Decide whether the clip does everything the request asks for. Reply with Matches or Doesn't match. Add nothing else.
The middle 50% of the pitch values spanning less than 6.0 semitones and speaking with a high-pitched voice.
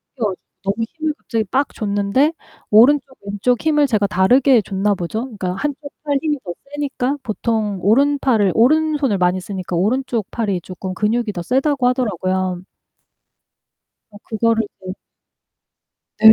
Matches